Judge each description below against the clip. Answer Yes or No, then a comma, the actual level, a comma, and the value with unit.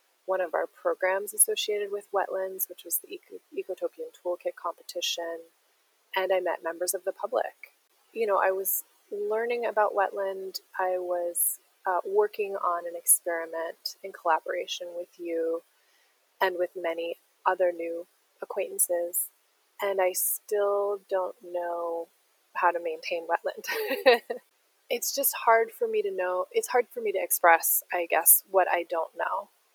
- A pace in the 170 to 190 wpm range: No, average, 145 wpm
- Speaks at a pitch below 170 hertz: No, high, 190 Hz